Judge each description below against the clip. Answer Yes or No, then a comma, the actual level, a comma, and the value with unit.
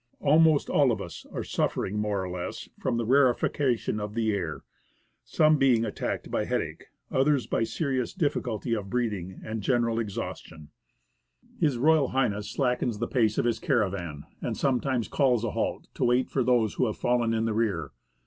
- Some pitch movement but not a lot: Yes, average, 3.7 semitones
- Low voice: Yes, low, 115 Hz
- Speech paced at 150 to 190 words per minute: Yes, average, 170 wpm